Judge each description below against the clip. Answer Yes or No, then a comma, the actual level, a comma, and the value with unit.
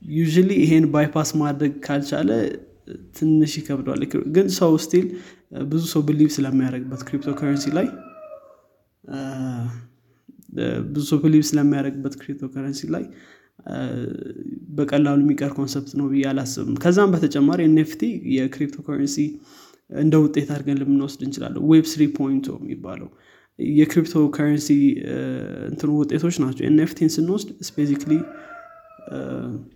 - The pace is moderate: Yes, average, 85 wpm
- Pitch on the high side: No, medium, 150 Hz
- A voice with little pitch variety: Yes, narrow, 2.1 semitones